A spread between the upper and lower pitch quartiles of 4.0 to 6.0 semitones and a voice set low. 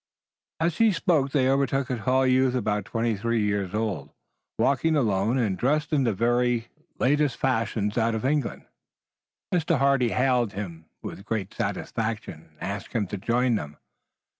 Yes: average, 4.3 semitones; low, 120 Hz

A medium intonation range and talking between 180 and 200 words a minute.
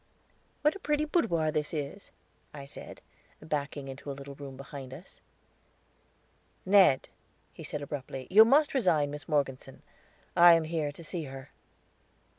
No: average, 4.1 semitones; average, 145 wpm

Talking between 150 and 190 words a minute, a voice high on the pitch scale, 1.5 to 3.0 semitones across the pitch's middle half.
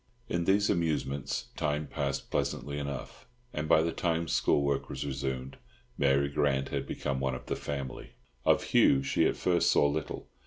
No: average, 170 wpm; very low, 70 Hz; narrow, 2.5 semitones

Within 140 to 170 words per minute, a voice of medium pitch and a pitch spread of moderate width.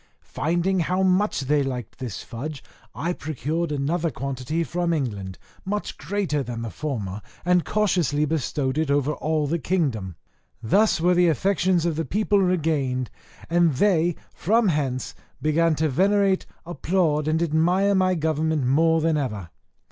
Yes: average, 150 wpm; medium, 160 Hz; average, 4.4 semitones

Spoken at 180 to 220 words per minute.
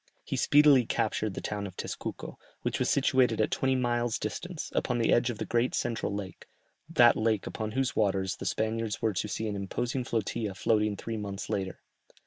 Yes: average, 190 wpm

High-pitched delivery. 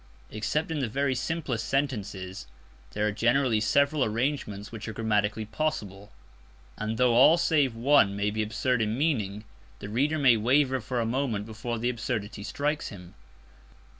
No: low, 115 Hz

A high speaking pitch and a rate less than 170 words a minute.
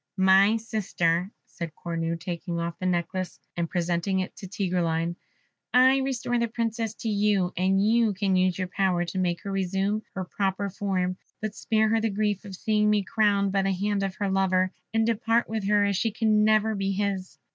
No: high, 195 Hz; average, 195 wpm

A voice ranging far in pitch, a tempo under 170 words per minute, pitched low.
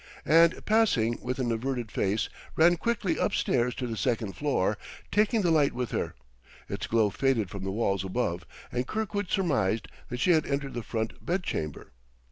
No: wide, 7.0 semitones; average, 175 wpm; low, 125 Hz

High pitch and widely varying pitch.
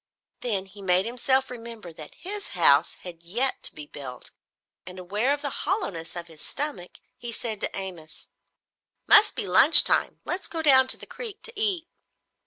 Yes: high, 230 Hz; wide, 8.5 semitones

